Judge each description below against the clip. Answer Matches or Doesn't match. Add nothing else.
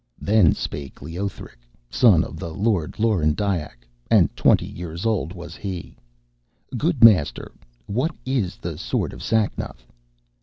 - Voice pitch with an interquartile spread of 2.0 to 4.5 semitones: Doesn't match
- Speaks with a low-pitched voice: Matches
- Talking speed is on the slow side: Matches